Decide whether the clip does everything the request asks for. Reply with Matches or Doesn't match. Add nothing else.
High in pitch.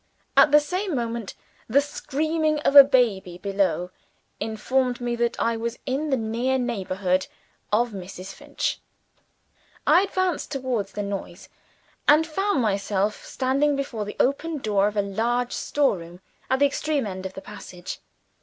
Matches